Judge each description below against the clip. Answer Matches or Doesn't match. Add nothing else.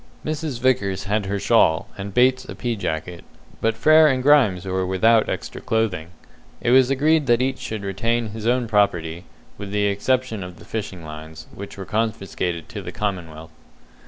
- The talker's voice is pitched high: Doesn't match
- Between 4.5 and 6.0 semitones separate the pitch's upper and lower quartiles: Matches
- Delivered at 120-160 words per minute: Doesn't match